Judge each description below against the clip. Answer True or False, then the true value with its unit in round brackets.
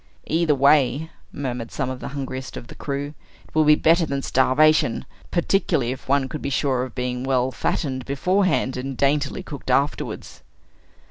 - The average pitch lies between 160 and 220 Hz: False (140 Hz)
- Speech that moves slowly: False (165 wpm)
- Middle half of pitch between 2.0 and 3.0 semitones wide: True (2.5 semitones)